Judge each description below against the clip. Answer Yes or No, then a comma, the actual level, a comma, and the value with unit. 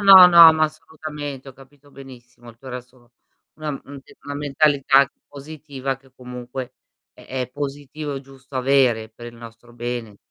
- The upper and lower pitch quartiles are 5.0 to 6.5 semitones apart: No, average, 2.8 semitones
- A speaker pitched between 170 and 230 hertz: No, low, 135 Hz